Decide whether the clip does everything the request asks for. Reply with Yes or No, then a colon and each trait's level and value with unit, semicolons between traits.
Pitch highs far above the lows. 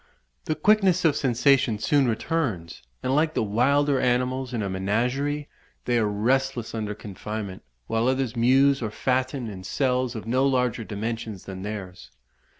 No: average, 4.1 semitones